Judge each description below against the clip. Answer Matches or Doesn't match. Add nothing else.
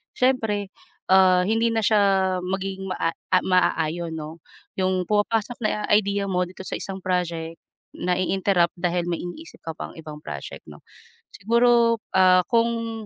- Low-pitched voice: Doesn't match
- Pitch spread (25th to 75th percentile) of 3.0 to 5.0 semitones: Matches